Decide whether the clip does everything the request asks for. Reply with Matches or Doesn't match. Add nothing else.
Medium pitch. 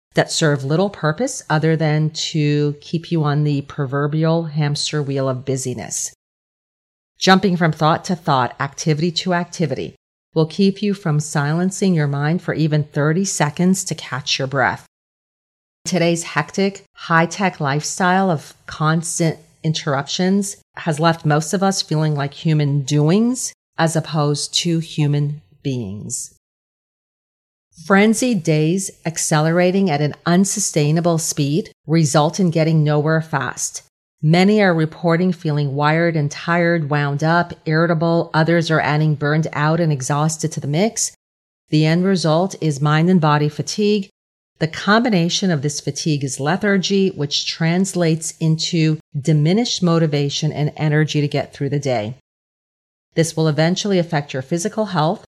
Matches